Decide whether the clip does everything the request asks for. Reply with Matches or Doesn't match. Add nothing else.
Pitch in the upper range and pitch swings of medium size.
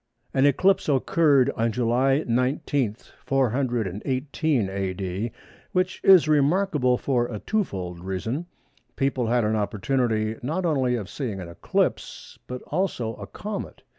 Doesn't match